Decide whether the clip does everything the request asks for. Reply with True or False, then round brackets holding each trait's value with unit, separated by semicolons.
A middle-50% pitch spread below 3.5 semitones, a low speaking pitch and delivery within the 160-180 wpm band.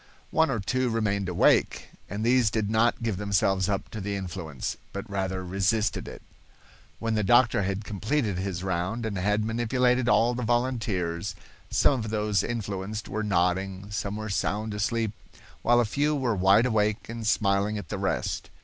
True (3.0 semitones; 105 Hz; 170 wpm)